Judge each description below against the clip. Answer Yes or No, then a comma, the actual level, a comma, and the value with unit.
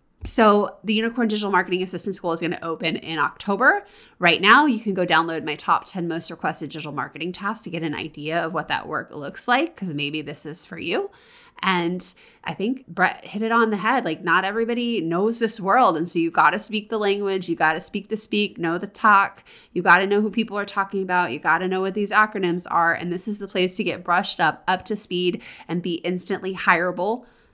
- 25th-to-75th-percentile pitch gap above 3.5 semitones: Yes, average, 4.1 semitones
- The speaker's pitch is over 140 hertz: Yes, medium, 185 Hz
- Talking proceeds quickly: Yes, fast, 230 wpm